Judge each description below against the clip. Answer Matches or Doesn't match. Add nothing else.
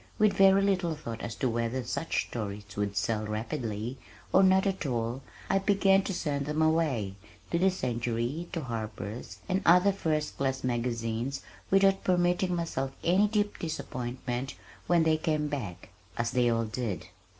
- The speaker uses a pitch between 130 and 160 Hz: Matches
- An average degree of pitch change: Doesn't match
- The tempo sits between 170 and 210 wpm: Doesn't match